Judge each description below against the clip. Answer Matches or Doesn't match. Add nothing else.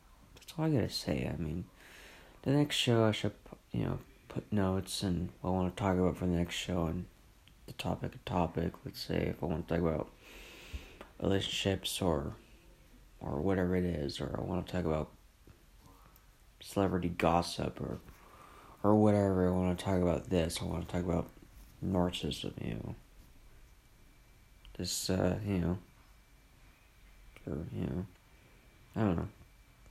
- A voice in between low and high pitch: Doesn't match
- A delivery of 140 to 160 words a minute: Matches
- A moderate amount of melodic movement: Doesn't match